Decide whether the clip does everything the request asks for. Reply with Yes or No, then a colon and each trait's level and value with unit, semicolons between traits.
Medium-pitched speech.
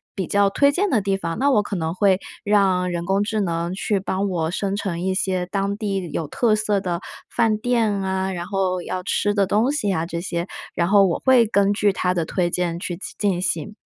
No: high, 195 Hz